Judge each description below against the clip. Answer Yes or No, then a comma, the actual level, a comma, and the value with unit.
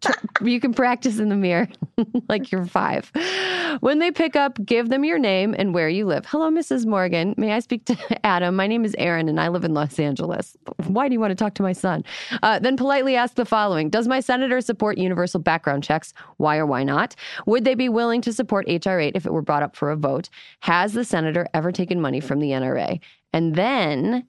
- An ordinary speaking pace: No, fast, 225 wpm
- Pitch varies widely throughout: Yes, wide, 6.2 semitones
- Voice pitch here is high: Yes, high, 210 Hz